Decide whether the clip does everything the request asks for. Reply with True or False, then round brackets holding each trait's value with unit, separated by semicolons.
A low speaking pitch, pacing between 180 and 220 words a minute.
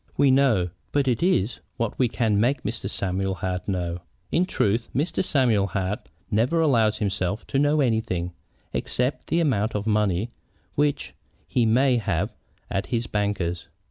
False (110 Hz; 155 wpm)